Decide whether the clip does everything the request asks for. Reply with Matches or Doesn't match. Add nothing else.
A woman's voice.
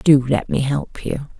Matches